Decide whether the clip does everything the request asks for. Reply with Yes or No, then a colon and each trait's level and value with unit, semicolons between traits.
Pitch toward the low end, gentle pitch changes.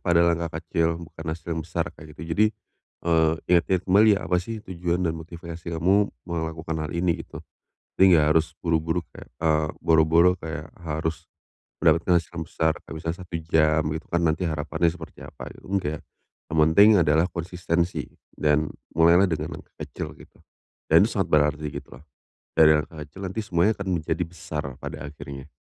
Yes: very low, 80 Hz; narrow, 1.8 semitones